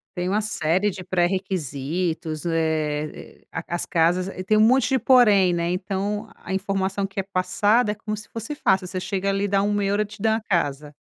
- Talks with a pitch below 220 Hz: Yes, high, 190 Hz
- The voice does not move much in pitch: No, average, 3.0 semitones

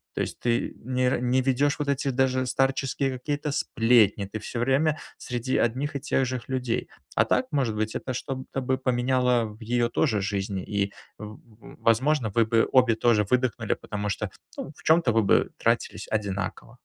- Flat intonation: No, average, 3.2 semitones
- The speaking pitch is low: Yes, low, 125 Hz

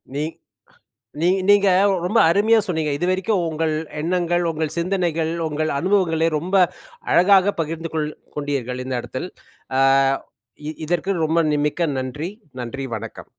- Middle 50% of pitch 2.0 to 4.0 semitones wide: Yes, average, 3.4 semitones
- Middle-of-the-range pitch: Yes, medium, 165 Hz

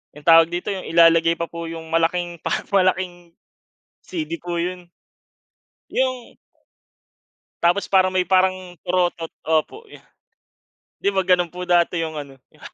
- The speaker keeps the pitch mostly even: Yes, narrow, 1.8 semitones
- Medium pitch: Yes, medium, 175 Hz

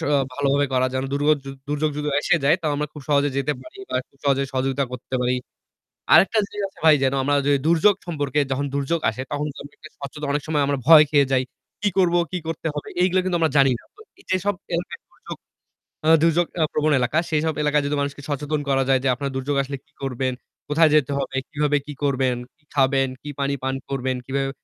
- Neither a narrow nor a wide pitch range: No, narrow, 2.3 semitones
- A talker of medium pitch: Yes, medium, 145 Hz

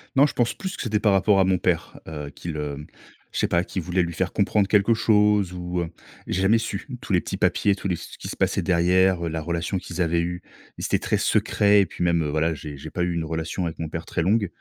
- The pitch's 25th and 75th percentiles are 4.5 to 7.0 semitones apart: No, average, 3.1 semitones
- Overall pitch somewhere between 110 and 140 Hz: No, very low, 90 Hz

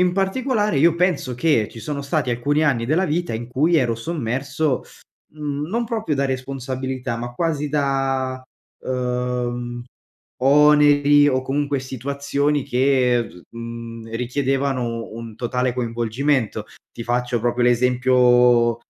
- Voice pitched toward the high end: No, low, 130 Hz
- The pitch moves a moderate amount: Yes, average, 3.2 semitones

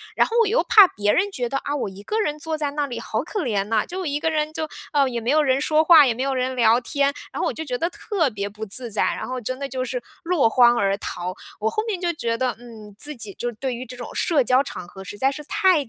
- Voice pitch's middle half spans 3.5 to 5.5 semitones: Yes, average, 5.0 semitones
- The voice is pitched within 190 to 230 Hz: No, very high, 260 Hz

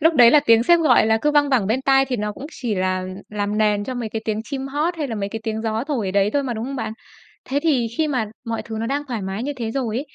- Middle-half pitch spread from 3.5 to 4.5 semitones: Yes, average, 4.2 semitones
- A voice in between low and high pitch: No, high, 235 Hz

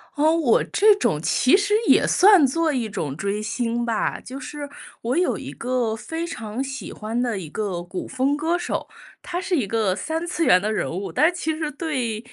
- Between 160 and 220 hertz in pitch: No, very high, 255 Hz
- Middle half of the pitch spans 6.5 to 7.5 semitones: Yes, wide, 7.0 semitones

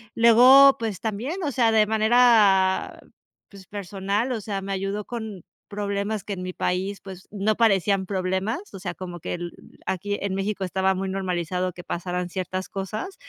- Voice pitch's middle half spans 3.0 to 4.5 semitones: No, narrow, 2.6 semitones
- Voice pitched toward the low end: No, high, 195 Hz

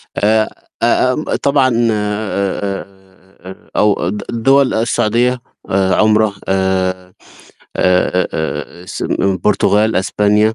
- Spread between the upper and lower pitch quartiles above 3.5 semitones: No, average, 2.8 semitones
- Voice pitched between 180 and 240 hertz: No, low, 105 Hz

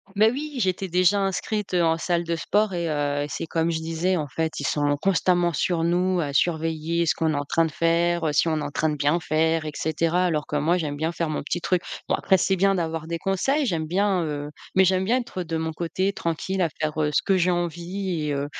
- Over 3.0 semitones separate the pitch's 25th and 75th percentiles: No, average, 2.7 semitones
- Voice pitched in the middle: Yes, medium, 170 Hz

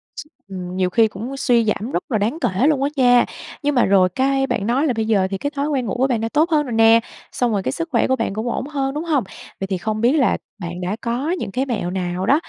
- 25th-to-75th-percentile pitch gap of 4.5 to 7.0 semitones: Yes, wide, 5.4 semitones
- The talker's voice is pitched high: Yes, high, 235 Hz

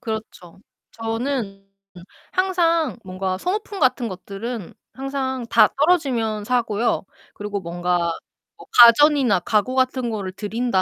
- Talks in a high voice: Yes, high, 230 Hz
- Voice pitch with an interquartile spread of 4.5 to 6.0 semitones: Yes, average, 5.1 semitones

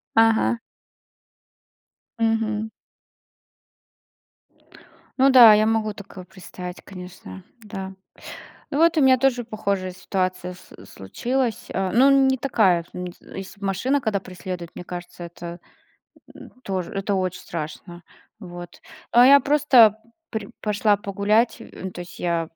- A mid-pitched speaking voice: No, high, 200 Hz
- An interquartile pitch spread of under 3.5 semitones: No, average, 3.9 semitones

